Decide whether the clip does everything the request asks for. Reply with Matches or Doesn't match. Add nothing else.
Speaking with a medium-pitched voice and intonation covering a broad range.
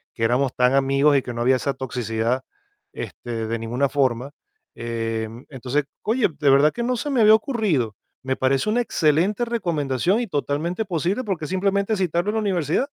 Matches